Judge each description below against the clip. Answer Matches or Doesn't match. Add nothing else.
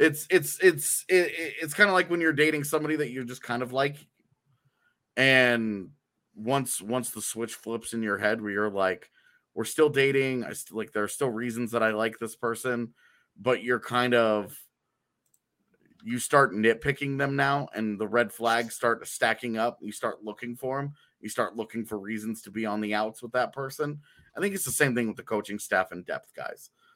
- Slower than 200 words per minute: Doesn't match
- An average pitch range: Matches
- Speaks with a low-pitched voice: Matches